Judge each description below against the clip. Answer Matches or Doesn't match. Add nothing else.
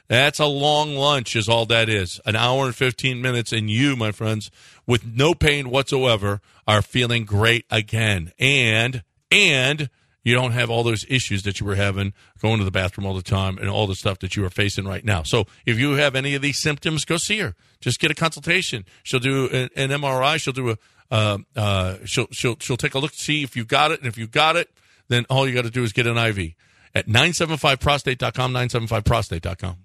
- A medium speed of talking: Doesn't match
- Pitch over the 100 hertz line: Matches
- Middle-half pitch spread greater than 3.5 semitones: Matches